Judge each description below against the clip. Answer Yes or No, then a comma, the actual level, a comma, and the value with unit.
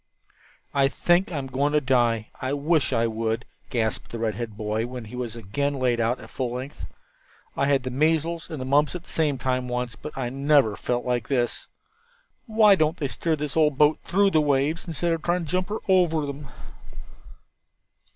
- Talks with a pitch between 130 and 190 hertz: Yes, medium, 140 Hz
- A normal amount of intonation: Yes, average, 4.3 semitones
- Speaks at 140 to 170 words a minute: No, average, 200 wpm